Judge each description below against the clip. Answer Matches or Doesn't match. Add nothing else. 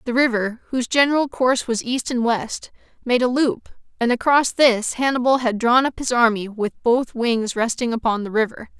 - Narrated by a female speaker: Matches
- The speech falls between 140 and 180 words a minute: Doesn't match